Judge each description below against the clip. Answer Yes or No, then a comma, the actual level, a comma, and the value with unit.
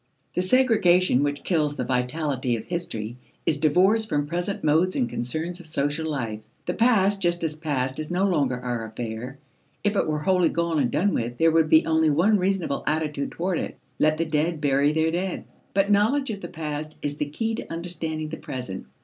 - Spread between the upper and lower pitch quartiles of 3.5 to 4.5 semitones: Yes, average, 4.0 semitones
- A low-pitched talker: No, medium, 160 Hz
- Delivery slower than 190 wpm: No, average, 200 wpm